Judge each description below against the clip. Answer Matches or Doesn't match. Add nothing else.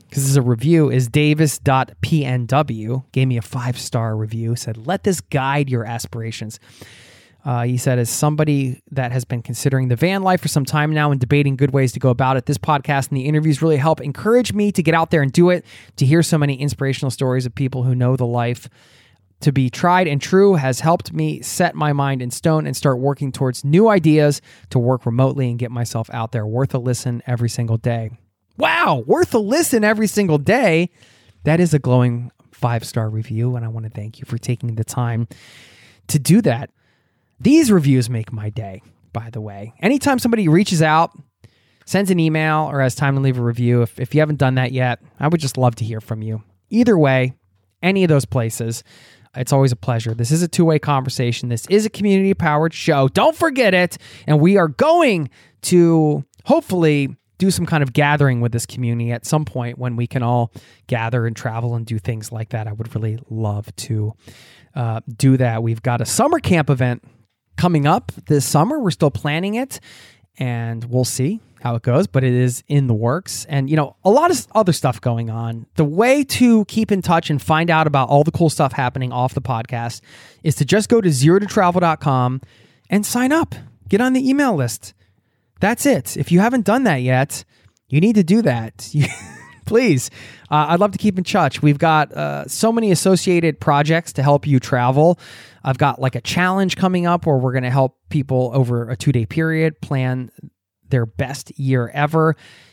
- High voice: Doesn't match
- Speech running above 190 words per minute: Matches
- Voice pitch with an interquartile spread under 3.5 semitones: Doesn't match